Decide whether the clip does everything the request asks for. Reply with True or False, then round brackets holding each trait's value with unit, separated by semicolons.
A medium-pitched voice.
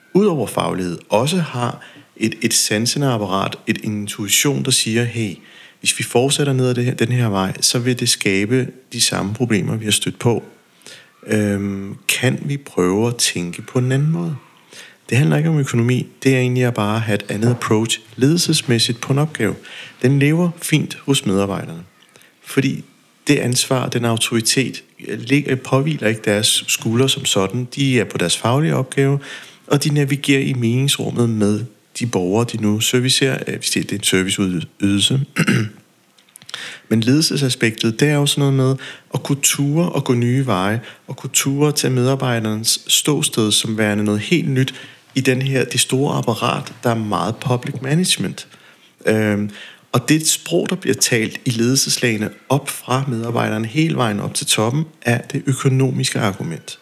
False (125 Hz)